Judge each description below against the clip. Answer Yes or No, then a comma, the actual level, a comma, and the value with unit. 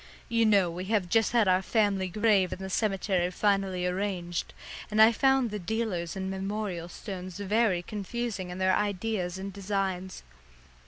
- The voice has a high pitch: Yes, high, 195 Hz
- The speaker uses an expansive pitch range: No, average, 2.7 semitones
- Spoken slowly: No, average, 160 wpm